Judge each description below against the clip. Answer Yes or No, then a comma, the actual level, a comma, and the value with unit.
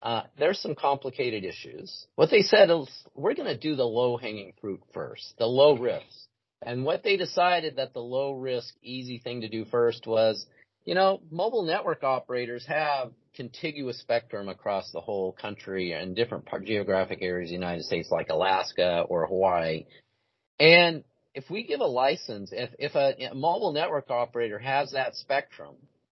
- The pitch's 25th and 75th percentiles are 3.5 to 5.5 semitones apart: Yes, average, 4.3 semitones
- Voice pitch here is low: Yes, low, 125 Hz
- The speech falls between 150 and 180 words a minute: Yes, average, 170 wpm